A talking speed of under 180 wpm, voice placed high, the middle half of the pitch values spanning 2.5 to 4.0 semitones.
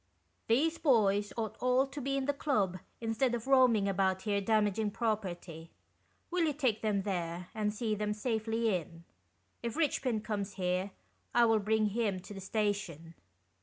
Yes: average, 170 wpm; high, 215 Hz; average, 3.4 semitones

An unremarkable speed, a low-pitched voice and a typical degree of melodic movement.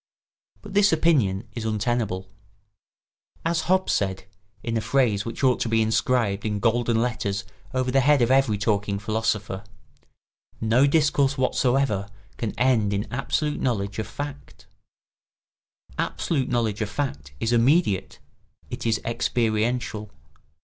No: slow, 130 wpm; low, 115 Hz; average, 4.0 semitones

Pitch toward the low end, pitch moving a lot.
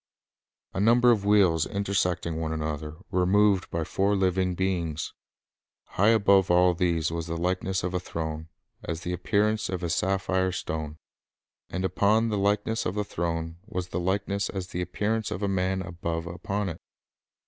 No: very low, 90 Hz; average, 3.0 semitones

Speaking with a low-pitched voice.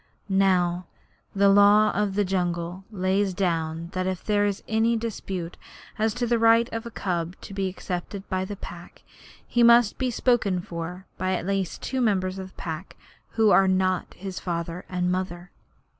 No: high, 190 Hz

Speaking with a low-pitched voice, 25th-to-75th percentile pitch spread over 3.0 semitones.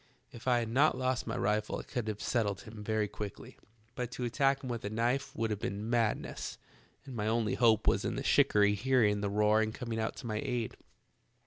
No: low, 115 Hz; narrow, 2.6 semitones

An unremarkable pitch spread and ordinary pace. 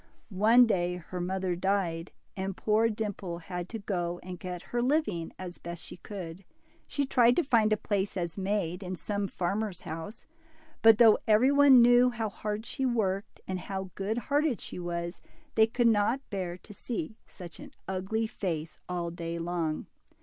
Yes: average, 4.1 semitones; average, 175 wpm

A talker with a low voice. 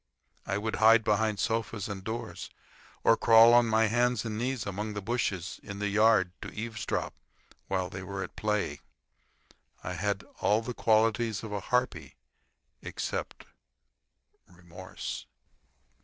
Yes: low, 110 Hz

